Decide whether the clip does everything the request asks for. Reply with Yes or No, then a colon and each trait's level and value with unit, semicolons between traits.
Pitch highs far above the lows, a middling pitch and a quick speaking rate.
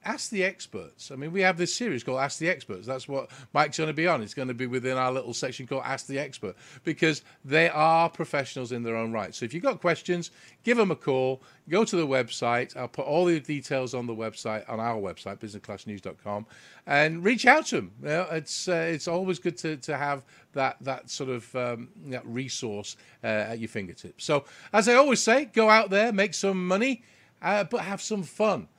Yes: wide, 6.3 semitones; medium, 145 Hz; fast, 225 wpm